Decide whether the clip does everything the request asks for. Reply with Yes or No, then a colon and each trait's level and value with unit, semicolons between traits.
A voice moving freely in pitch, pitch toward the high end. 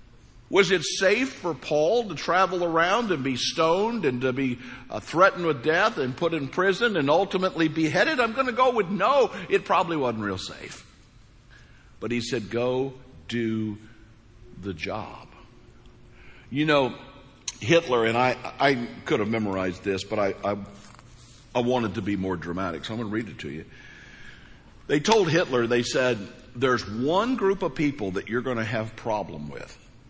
No: wide, 6.7 semitones; low, 125 Hz